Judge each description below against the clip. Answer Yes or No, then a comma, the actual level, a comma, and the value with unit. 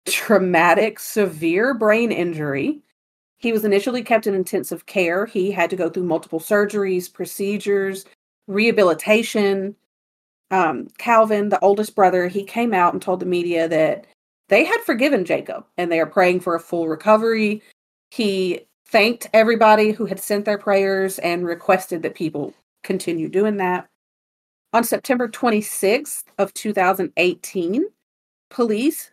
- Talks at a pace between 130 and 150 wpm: Yes, slow, 135 wpm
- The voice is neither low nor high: No, high, 200 Hz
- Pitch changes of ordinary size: Yes, average, 3.2 semitones